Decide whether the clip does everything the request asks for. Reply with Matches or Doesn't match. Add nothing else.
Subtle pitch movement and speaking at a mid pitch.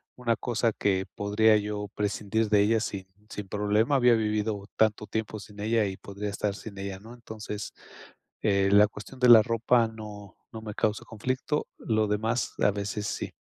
Doesn't match